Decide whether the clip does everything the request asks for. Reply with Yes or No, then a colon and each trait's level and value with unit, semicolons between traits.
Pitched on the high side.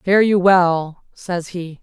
No: medium, 180 Hz